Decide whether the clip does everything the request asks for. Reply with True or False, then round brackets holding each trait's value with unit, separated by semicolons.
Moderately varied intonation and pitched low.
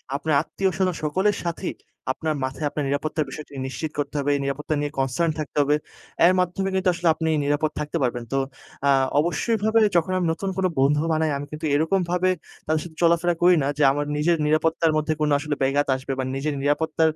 False (3.0 semitones; 155 Hz)